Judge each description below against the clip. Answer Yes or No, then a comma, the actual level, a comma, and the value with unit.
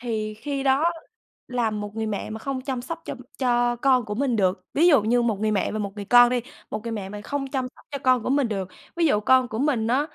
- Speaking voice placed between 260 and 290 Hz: No, high, 240 Hz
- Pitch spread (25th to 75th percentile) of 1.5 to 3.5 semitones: No, average, 3.9 semitones